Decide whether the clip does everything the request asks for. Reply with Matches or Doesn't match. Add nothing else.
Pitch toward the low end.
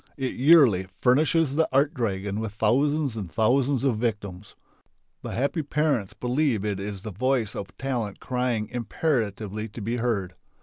Matches